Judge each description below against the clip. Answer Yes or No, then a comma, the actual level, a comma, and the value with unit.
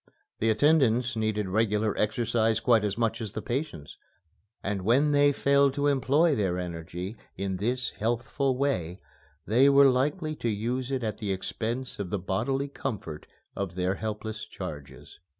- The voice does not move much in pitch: No, average, 5.2 semitones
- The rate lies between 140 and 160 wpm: Yes, average, 155 wpm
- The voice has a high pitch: No, low, 115 Hz